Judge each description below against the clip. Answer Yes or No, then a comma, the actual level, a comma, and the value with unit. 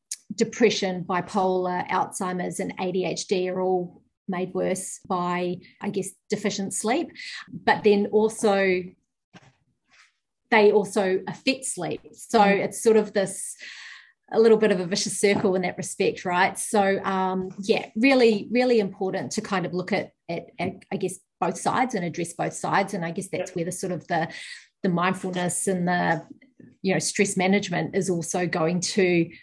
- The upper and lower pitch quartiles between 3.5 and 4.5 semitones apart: No, narrow, 2.6 semitones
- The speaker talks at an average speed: Yes, average, 160 wpm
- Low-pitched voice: No, high, 195 Hz